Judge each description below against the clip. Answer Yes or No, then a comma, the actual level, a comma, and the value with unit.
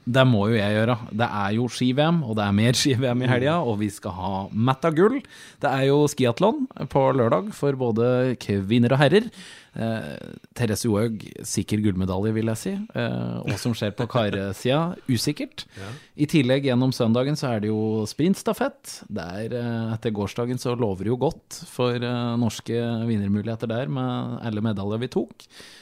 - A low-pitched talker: Yes, low, 120 Hz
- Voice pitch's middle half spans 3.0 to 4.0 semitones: Yes, average, 3.7 semitones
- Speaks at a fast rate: No, average, 175 wpm